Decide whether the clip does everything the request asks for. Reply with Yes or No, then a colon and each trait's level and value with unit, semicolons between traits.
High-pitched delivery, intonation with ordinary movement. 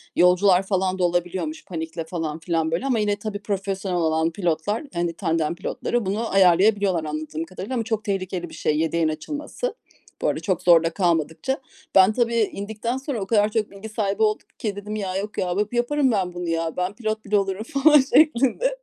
Yes: high, 195 Hz; average, 4.3 semitones